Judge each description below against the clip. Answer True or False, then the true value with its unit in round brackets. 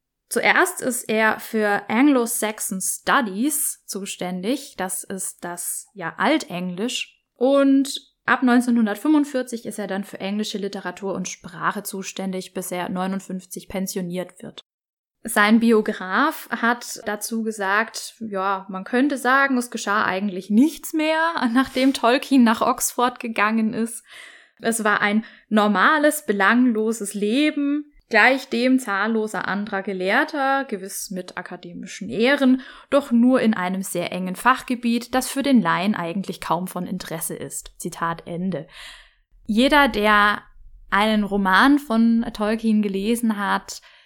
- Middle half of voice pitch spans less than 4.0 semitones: False (4.7 semitones)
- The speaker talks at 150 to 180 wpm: False (125 wpm)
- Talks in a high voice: True (220 Hz)